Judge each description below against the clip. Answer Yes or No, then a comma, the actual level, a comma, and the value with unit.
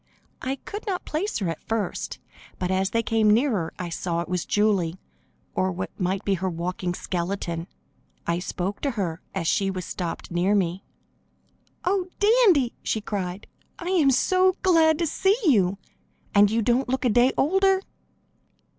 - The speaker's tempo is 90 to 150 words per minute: No, average, 165 wpm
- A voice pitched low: No, high, 205 Hz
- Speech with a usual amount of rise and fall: No, wide, 7.4 semitones